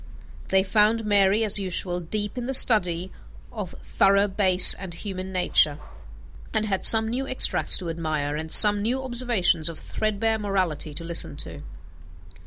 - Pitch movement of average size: Yes, average, 3.7 semitones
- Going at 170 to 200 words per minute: No, average, 155 wpm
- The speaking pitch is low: No, high, 195 Hz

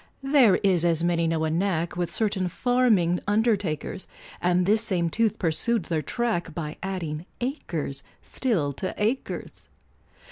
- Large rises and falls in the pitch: No, average, 4.8 semitones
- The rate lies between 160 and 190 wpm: No, average, 140 wpm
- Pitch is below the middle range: No, medium, 180 Hz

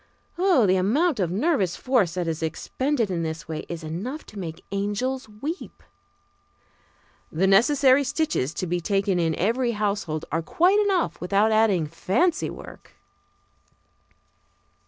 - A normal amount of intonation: No, wide, 7.3 semitones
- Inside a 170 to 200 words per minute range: No, slow, 135 wpm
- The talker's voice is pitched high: Yes, high, 205 Hz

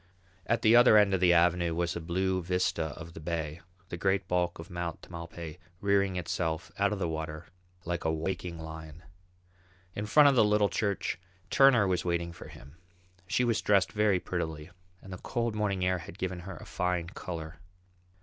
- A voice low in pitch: Yes, very low, 90 Hz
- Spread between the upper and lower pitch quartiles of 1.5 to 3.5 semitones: Yes, average, 3.0 semitones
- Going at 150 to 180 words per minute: No, average, 190 wpm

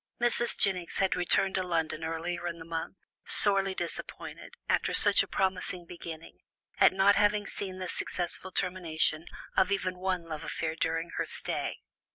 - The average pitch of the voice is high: No, medium, 180 Hz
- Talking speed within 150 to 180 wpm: Yes, average, 160 wpm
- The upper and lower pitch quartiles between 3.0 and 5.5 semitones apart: No, narrow, 2.5 semitones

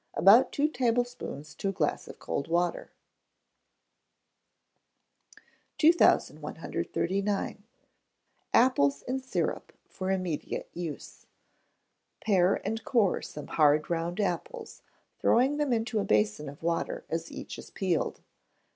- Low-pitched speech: No, high, 190 Hz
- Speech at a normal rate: No, slow, 110 wpm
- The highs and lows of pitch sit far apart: Yes, wide, 6.6 semitones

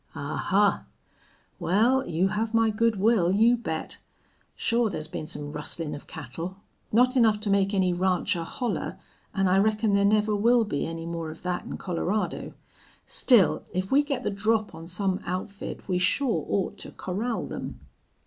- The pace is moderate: Yes, average, 170 wpm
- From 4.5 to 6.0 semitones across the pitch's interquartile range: No, average, 4.0 semitones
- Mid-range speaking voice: No, high, 200 Hz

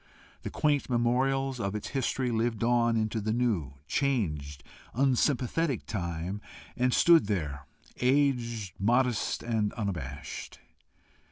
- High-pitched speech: No, low, 115 Hz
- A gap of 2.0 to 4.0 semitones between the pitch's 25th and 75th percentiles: No, average, 4.5 semitones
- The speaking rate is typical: No, slow, 110 wpm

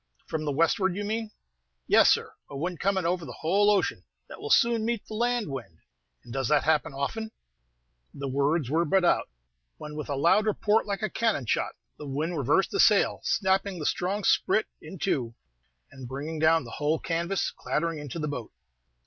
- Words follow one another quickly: No, average, 190 wpm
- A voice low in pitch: No, medium, 165 Hz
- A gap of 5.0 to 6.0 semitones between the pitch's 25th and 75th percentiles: Yes, wide, 5.6 semitones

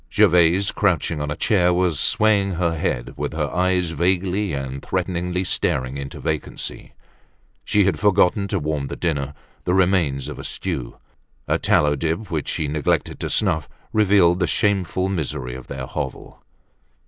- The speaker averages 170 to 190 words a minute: No, average, 160 wpm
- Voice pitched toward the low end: Yes, very low, 85 Hz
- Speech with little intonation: No, average, 4.3 semitones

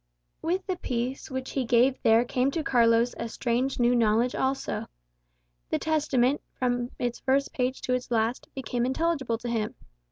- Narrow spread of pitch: Yes, narrow, 2.1 semitones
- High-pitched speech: Yes, very high, 250 Hz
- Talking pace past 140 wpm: Yes, average, 165 wpm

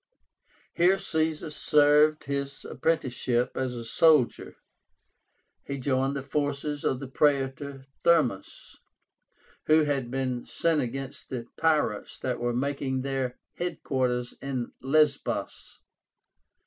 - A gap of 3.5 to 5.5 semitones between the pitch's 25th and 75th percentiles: No, average, 2.7 semitones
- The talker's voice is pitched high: No, medium, 140 Hz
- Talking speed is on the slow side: Yes, slow, 110 wpm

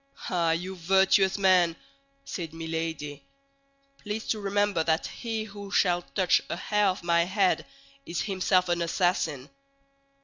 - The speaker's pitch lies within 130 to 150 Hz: No, medium, 185 Hz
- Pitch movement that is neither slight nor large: Yes, average, 3.0 semitones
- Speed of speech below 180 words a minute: Yes, slow, 135 wpm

